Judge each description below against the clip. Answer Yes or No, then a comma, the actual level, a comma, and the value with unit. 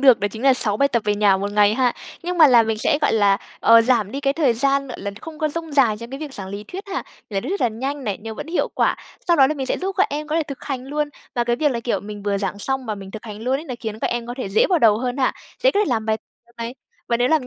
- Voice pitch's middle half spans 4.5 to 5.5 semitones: Yes, average, 4.8 semitones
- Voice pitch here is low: No, high, 245 Hz